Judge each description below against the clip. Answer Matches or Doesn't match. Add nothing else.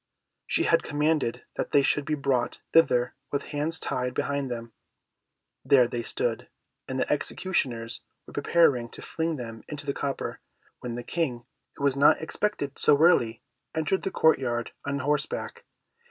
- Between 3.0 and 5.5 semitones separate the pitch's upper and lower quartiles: Matches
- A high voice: Doesn't match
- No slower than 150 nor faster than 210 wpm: Matches